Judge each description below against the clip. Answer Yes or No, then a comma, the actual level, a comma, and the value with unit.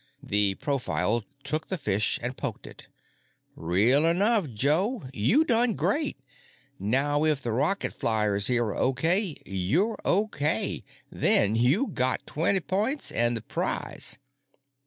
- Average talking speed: No, slow, 130 wpm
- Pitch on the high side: No, medium, 140 Hz